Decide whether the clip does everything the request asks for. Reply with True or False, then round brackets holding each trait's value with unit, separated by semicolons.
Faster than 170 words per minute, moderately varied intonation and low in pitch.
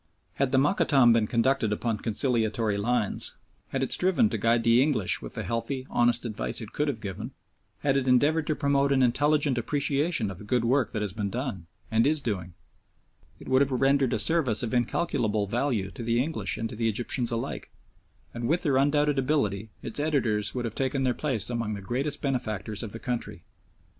True (200 wpm; 3.9 semitones; 120 Hz)